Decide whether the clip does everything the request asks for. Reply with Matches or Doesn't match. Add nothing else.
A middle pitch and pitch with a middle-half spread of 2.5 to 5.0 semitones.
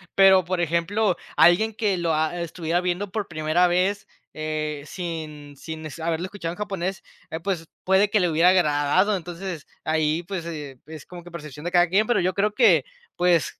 Matches